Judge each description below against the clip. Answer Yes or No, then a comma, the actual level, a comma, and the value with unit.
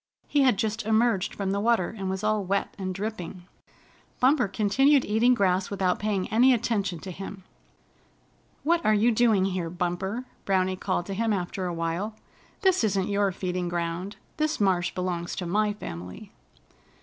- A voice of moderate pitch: No, high, 195 Hz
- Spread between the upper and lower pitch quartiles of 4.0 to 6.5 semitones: No, average, 3.2 semitones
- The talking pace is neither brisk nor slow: Yes, average, 165 wpm